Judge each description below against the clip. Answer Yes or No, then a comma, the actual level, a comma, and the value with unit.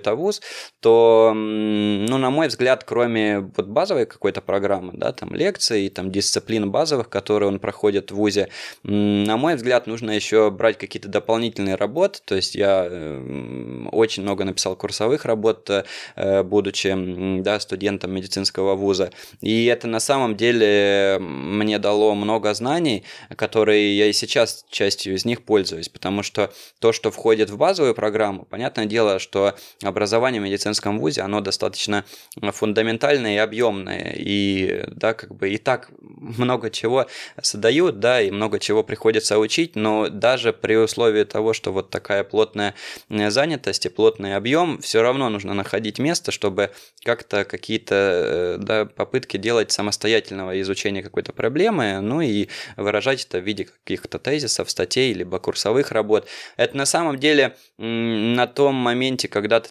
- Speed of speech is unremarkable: Yes, average, 145 wpm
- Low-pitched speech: Yes, low, 105 Hz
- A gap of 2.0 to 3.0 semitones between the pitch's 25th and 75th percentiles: Yes, narrow, 2.4 semitones